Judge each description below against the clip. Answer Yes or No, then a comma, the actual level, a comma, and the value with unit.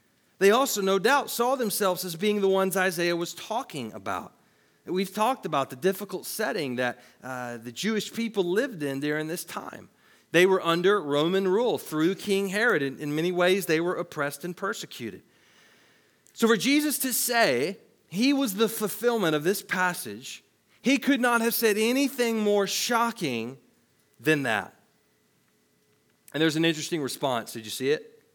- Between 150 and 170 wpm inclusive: Yes, average, 165 wpm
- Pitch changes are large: Yes, wide, 5.8 semitones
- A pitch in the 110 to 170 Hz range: No, high, 190 Hz